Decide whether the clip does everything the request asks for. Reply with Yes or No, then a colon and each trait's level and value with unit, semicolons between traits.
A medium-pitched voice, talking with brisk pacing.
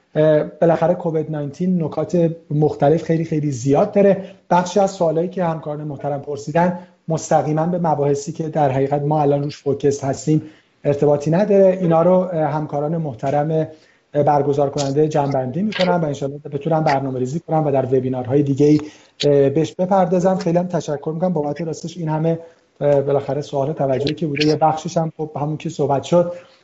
Yes: medium, 155 Hz; fast, 160 wpm